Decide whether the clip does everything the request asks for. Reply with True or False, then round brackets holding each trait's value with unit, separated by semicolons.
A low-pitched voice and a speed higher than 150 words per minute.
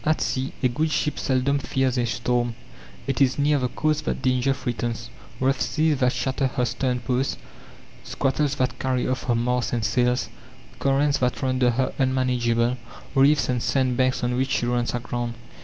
True (130 Hz; 175 wpm)